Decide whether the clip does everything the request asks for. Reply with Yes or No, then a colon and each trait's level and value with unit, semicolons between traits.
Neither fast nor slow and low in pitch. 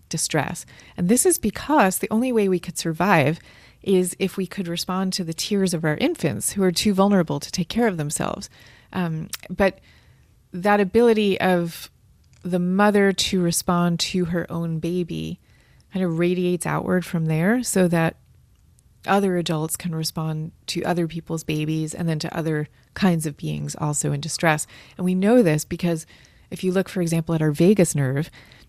No: average, 175 wpm; medium, 175 Hz